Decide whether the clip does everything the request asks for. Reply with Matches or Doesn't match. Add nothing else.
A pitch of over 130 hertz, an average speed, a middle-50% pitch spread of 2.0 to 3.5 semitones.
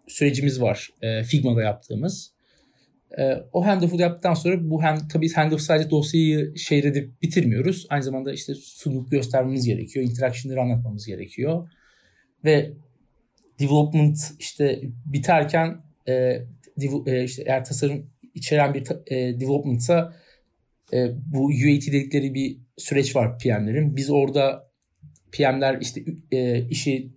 Matches